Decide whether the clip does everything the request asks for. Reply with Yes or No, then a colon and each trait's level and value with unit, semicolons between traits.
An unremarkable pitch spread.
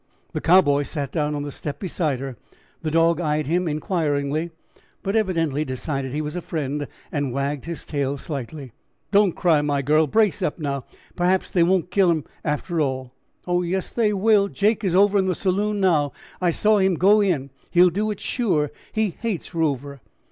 Yes: average, 4.7 semitones